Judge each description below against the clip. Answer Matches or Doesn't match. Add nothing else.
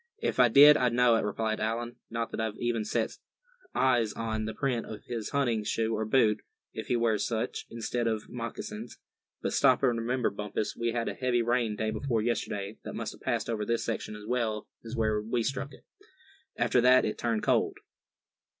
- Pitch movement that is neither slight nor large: Doesn't match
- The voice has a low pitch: Matches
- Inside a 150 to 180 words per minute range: Doesn't match